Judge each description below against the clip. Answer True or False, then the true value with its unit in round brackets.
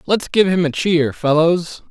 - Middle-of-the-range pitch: True (170 Hz)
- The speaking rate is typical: True (190 wpm)